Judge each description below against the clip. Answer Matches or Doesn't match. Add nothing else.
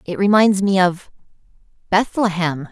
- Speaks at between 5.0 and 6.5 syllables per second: Doesn't match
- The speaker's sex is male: Doesn't match